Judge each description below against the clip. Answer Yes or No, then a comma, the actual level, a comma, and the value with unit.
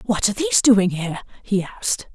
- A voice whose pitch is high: Yes, high, 205 Hz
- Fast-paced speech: No, average, 195 wpm